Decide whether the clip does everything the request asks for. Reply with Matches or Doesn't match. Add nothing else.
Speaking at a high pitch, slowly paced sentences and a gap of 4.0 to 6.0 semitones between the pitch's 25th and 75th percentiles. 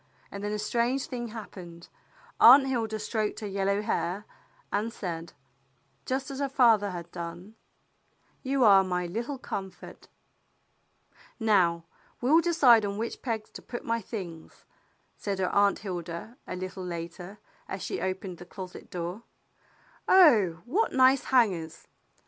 Doesn't match